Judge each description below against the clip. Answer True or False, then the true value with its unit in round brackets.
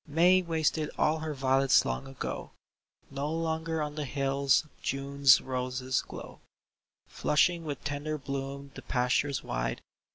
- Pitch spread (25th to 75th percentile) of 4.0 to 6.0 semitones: False (2.5 semitones)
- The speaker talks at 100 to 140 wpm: True (135 wpm)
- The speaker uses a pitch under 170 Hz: True (140 Hz)